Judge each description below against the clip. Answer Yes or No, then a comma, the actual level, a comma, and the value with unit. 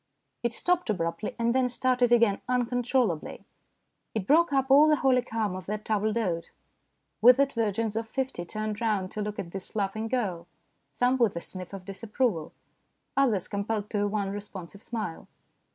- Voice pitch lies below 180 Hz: No, high, 220 Hz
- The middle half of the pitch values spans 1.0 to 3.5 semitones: No, average, 3.9 semitones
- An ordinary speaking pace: Yes, average, 170 wpm